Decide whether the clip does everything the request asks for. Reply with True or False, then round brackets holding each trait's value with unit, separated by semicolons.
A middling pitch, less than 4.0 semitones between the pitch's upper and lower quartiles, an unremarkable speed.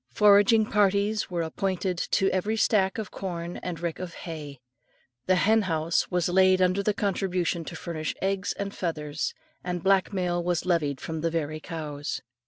True (180 Hz; 2.9 semitones; 160 wpm)